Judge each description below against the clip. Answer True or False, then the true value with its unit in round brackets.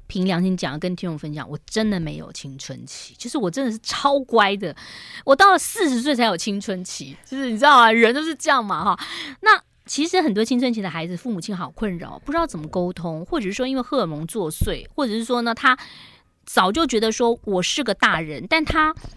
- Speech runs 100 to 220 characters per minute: False (330 characters per minute)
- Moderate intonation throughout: False (7.5 semitones)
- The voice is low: False (225 Hz)